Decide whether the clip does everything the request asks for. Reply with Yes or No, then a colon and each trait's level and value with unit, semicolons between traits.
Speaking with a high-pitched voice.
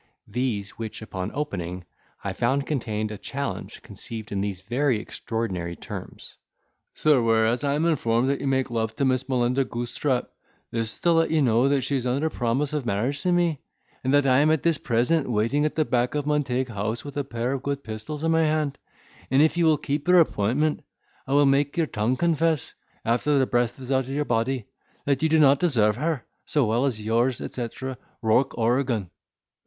No: low, 130 Hz